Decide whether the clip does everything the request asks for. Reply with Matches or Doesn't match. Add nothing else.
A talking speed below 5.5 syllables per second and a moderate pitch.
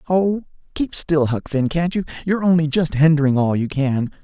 Matches